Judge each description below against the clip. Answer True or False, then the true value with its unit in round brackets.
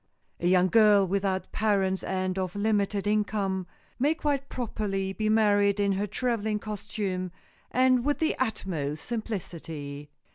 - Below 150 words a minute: True (135 wpm)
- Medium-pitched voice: False (205 Hz)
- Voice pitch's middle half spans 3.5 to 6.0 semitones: False (2.6 semitones)